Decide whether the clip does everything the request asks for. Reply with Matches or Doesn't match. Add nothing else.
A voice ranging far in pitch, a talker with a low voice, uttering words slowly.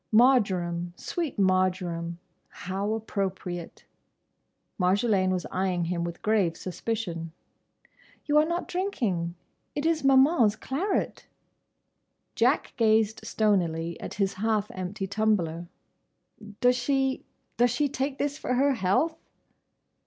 Doesn't match